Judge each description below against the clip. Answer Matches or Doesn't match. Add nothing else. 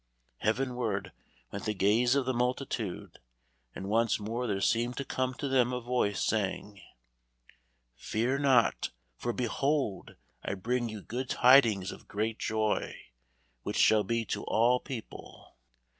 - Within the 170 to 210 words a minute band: Doesn't match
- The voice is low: Matches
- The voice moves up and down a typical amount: Matches